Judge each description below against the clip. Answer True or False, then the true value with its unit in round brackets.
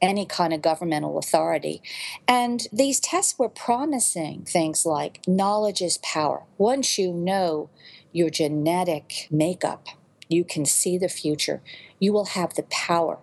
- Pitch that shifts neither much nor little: True (4.3 semitones)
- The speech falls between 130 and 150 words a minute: True (140 wpm)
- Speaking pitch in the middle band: True (175 Hz)